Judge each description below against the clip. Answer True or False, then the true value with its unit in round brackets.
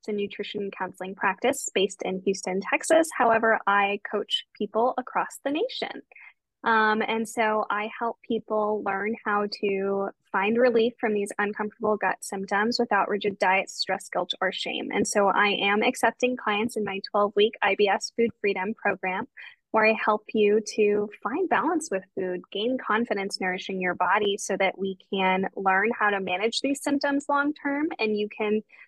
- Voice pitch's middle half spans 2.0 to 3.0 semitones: True (2.6 semitones)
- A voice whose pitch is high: True (210 Hz)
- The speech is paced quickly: False (165 wpm)